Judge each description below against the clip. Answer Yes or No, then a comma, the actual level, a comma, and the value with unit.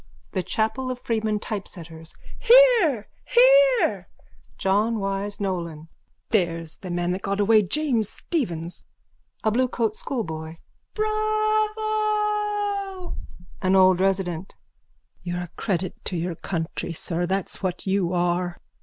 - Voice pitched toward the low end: No, high, 200 Hz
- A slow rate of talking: Yes, slow, 115 wpm